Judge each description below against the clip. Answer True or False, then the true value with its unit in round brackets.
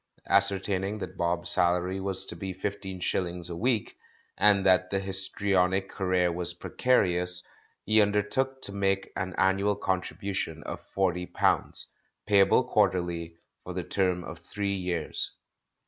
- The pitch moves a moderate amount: False (2.0 semitones)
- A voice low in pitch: True (95 Hz)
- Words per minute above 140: False (135 wpm)